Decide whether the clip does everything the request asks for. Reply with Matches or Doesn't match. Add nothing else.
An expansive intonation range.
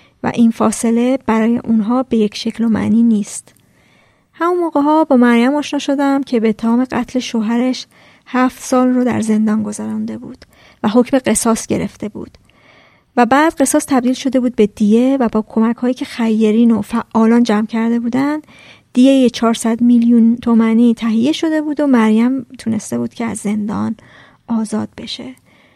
Doesn't match